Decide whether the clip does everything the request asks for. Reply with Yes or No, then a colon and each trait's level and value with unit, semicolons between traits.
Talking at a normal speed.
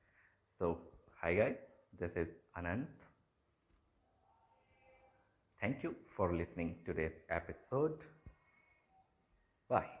No: slow, 80 wpm